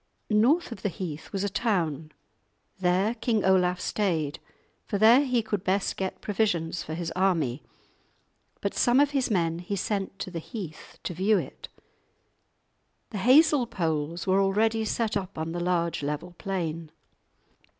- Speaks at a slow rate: No, average, 155 wpm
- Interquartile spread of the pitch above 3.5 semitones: Yes, average, 4.5 semitones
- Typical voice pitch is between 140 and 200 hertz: Yes, high, 190 Hz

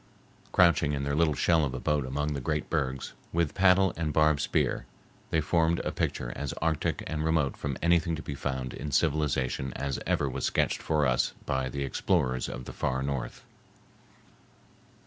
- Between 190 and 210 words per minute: No, average, 180 wpm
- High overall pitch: No, very low, 75 Hz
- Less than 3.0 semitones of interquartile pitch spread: No, average, 3.3 semitones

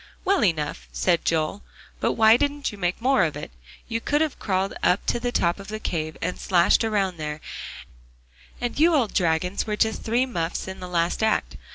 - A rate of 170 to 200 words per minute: Yes, average, 195 wpm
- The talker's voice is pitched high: Yes, high, 195 Hz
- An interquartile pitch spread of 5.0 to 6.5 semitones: Yes, wide, 5.5 semitones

